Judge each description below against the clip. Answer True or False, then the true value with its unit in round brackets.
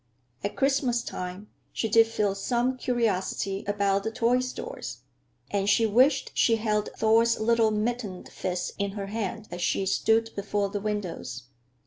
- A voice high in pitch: True (215 Hz)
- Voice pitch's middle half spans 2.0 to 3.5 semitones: True (2.8 semitones)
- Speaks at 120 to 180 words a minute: True (150 wpm)